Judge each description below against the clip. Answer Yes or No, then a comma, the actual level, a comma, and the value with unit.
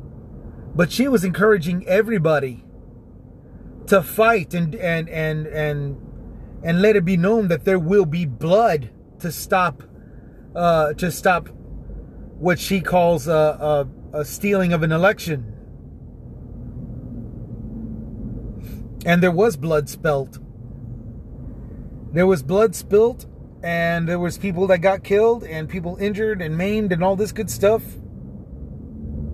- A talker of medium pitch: Yes, medium, 160 Hz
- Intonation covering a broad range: Yes, wide, 7.7 semitones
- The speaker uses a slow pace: Yes, slow, 125 wpm